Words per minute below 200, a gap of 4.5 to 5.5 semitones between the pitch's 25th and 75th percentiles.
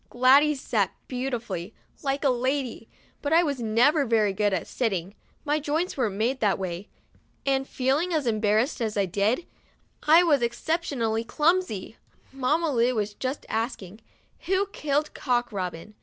Yes: average, 155 wpm; average, 5.1 semitones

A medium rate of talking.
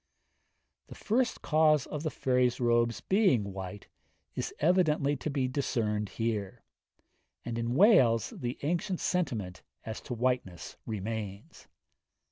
No: slow, 120 wpm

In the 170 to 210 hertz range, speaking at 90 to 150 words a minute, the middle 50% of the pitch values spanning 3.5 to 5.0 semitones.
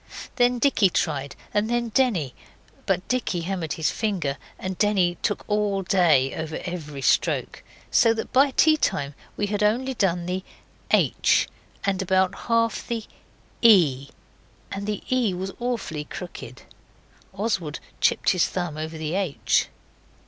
No: high, 190 Hz; average, 140 wpm; wide, 5.4 semitones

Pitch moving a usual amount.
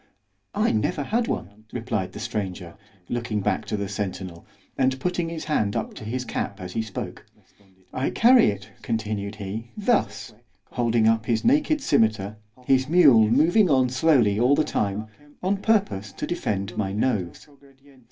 No: wide, 6.2 semitones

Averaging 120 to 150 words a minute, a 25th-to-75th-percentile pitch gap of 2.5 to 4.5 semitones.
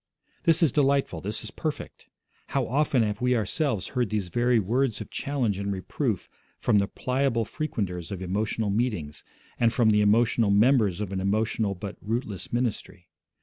No: average, 165 wpm; average, 4.0 semitones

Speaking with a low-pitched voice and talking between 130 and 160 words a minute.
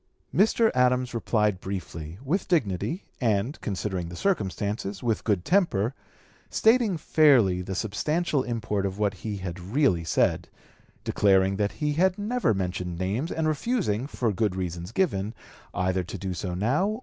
Yes: low, 105 Hz; average, 150 wpm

